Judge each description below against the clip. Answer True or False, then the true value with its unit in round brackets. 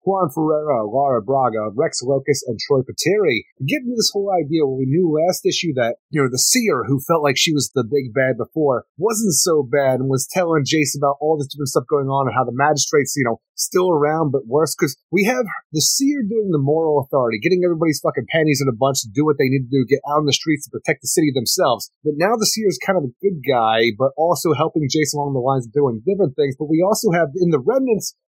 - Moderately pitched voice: True (150 Hz)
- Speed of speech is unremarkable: False (245 wpm)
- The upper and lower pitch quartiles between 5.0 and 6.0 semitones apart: False (4.3 semitones)